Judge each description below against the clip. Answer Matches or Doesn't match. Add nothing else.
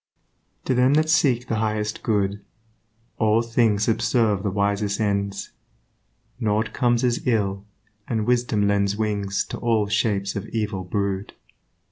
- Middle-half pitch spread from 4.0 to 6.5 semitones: Doesn't match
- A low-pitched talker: Matches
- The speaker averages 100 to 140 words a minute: Matches